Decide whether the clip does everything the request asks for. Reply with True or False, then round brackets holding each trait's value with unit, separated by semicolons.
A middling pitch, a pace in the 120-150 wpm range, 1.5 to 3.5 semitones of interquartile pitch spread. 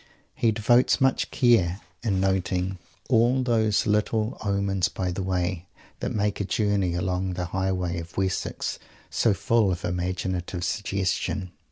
False (95 Hz; 145 wpm; 2.9 semitones)